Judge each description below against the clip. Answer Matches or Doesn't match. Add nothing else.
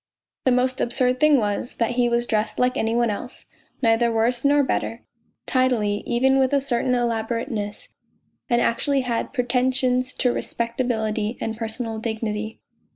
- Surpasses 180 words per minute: Doesn't match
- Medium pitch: Doesn't match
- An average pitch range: Doesn't match